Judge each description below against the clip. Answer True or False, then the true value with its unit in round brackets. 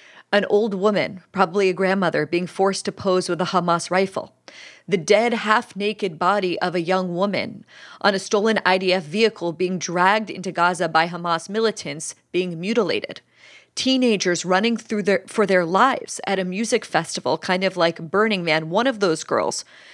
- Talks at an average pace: True (170 wpm)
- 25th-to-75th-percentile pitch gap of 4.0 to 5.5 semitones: False (2.8 semitones)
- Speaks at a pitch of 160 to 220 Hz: True (190 Hz)